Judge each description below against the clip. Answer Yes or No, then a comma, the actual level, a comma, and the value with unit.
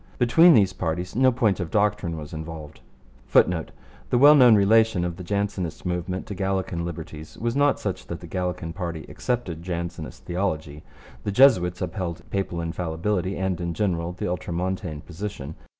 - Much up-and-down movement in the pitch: No, average, 3.5 semitones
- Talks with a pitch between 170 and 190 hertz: No, very low, 90 Hz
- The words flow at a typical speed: Yes, average, 160 wpm